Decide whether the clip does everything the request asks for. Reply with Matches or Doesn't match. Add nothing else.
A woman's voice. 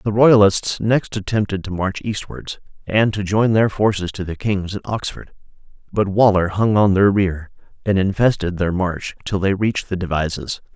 Doesn't match